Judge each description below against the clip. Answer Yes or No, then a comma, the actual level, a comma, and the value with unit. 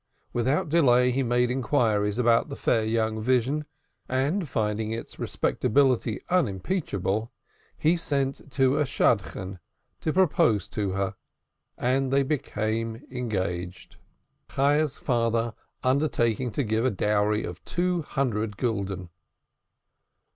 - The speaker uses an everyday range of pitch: Yes, average, 4.4 semitones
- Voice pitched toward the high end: No, low, 120 Hz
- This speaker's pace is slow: Yes, slow, 110 wpm